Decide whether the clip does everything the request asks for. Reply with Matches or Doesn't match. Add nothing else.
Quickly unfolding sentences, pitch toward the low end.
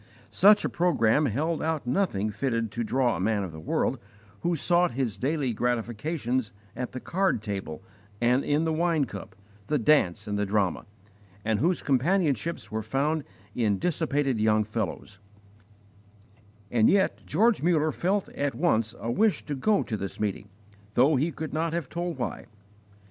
Doesn't match